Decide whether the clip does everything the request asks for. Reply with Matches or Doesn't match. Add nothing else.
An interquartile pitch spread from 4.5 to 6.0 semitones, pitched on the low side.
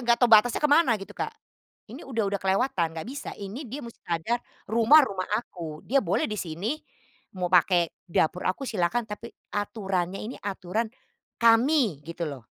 Doesn't match